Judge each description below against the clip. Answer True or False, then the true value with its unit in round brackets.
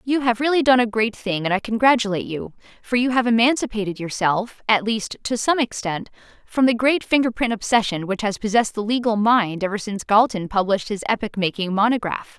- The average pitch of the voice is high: True (220 Hz)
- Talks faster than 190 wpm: True (200 wpm)